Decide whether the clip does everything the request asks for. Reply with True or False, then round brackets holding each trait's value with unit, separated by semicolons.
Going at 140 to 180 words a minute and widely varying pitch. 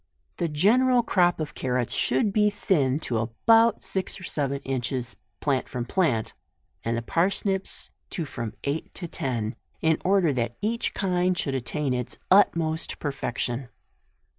True (155 wpm; 7.0 semitones)